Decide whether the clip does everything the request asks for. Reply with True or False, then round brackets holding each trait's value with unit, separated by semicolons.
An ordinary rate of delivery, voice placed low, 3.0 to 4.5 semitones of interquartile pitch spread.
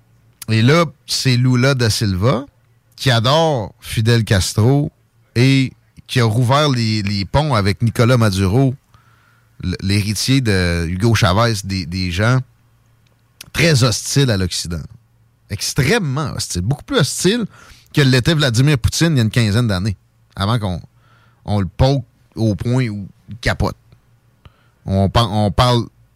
False (140 wpm; 120 Hz; 3.3 semitones)